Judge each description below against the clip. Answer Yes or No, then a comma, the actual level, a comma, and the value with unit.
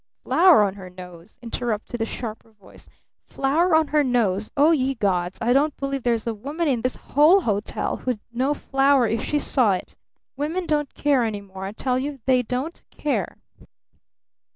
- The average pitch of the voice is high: Yes, very high, 255 Hz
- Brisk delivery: No, average, 175 wpm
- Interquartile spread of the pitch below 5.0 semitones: No, average, 5.3 semitones